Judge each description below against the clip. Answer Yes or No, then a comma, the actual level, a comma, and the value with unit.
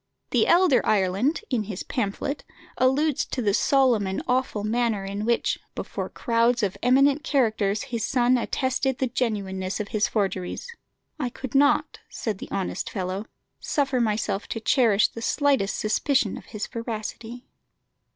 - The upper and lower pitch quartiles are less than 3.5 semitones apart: No, average, 4.1 semitones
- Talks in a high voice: Yes, high, 230 Hz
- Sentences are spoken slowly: No, average, 150 wpm